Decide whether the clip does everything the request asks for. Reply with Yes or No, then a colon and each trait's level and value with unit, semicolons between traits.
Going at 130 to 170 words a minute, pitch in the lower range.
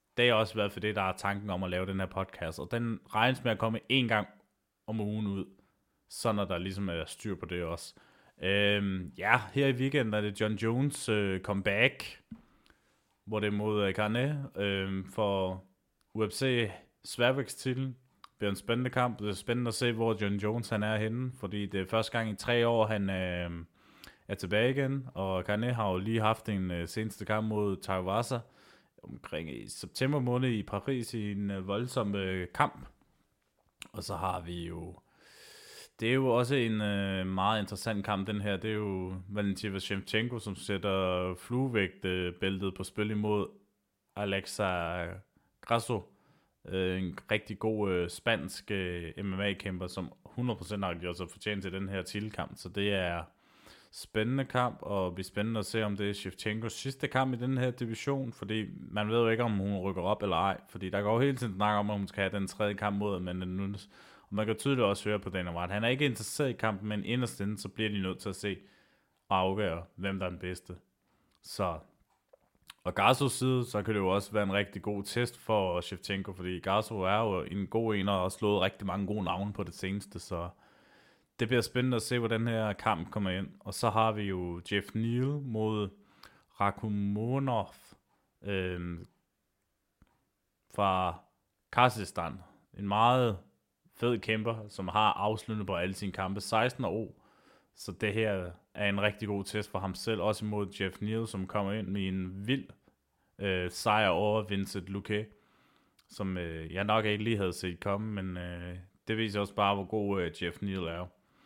No: average, 190 wpm; low, 100 Hz